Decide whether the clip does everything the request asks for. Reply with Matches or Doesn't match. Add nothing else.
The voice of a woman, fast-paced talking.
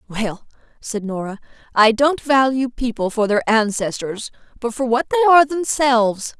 Doesn't match